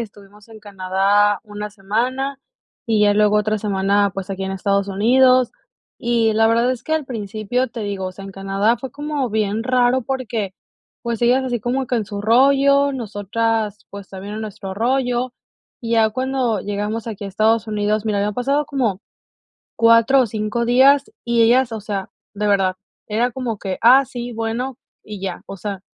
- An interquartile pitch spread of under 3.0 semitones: No, average, 3.3 semitones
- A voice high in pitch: Yes, high, 220 Hz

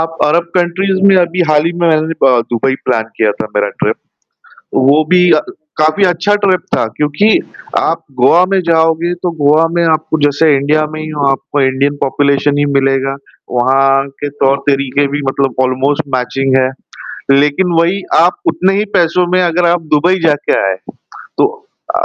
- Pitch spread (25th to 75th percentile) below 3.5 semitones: No, average, 4.1 semitones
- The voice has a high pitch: No, medium, 155 Hz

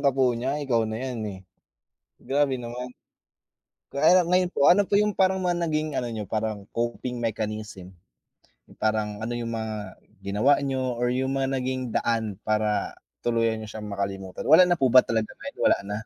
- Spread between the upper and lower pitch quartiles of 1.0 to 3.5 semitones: No, average, 4.0 semitones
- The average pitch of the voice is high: No, low, 120 Hz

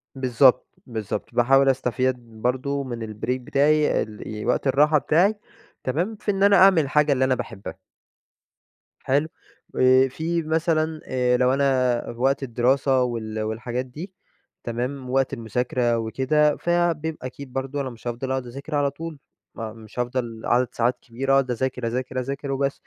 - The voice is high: No, low, 130 Hz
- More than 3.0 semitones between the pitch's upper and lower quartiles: No, average, 2.7 semitones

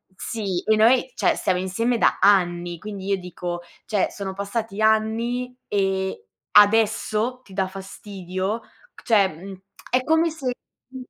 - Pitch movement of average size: Yes, average, 3.2 semitones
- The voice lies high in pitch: Yes, high, 205 Hz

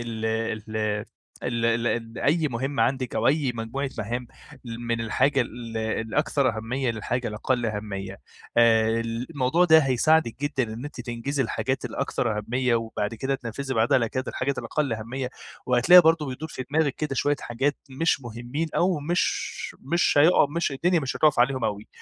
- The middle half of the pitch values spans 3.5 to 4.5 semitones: Yes, average, 3.8 semitones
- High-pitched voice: No, low, 125 Hz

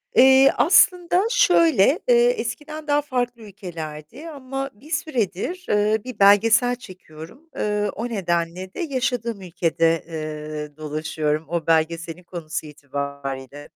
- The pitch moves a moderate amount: No, wide, 8.9 semitones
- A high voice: Yes, high, 205 Hz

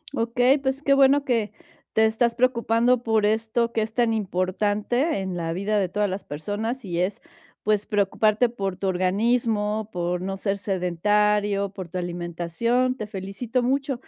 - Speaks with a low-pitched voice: No, high, 210 Hz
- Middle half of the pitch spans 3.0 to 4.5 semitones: Yes, average, 3.7 semitones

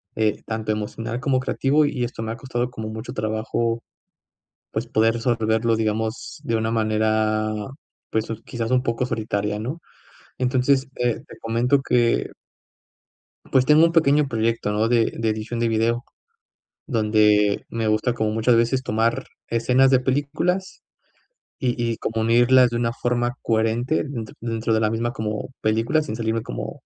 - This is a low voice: Yes, low, 115 Hz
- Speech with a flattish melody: Yes, narrow, 2.2 semitones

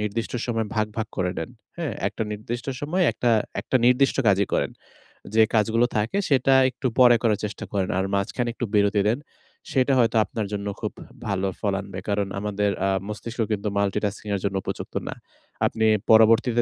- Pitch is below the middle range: Yes, low, 110 Hz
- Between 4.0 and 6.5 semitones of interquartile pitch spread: No, average, 2.9 semitones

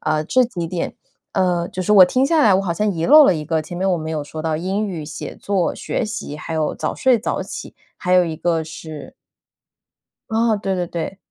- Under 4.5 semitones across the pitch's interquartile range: Yes, average, 4.1 semitones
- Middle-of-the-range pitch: Yes, medium, 180 Hz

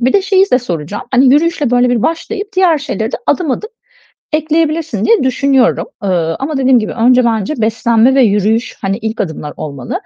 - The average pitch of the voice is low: No, very high, 250 Hz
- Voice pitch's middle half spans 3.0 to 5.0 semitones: No, wide, 5.5 semitones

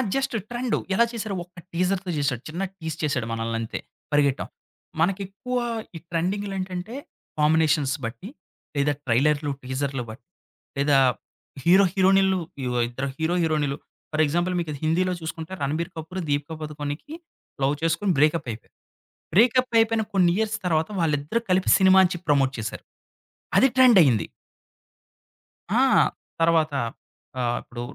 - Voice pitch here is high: No, medium, 160 Hz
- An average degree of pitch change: Yes, average, 4.9 semitones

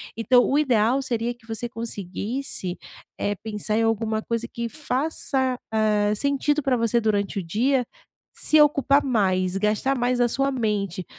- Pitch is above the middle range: Yes, high, 230 Hz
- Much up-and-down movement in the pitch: No, average, 3.8 semitones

